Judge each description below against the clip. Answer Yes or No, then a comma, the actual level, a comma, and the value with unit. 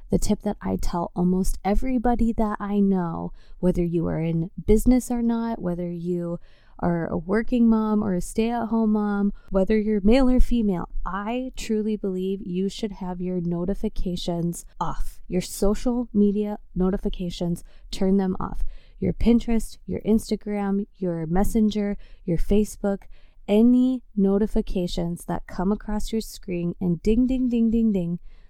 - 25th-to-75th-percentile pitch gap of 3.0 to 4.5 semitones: Yes, average, 3.6 semitones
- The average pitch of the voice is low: No, high, 205 Hz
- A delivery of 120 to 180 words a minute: Yes, average, 150 wpm